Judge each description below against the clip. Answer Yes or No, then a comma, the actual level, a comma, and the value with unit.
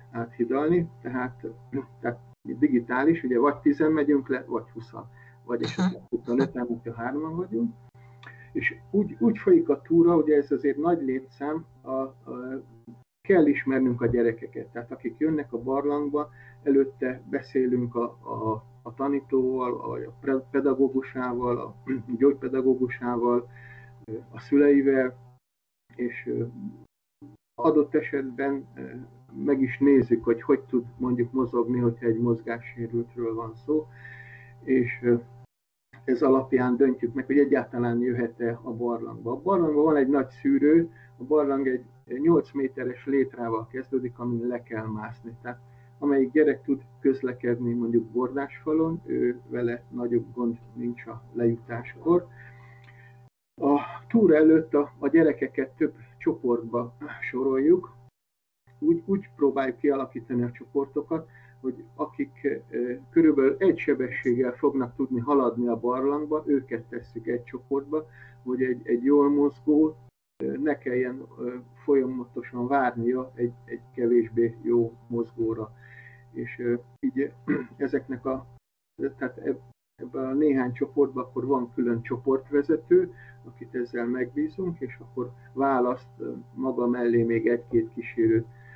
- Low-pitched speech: Yes, low, 130 Hz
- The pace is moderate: Yes, average, 125 wpm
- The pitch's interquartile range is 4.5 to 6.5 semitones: No, narrow, 2.5 semitones